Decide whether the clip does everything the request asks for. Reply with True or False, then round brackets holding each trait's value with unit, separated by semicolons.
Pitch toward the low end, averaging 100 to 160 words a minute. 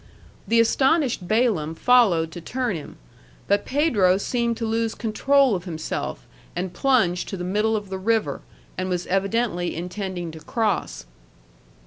False (205 Hz; 145 wpm)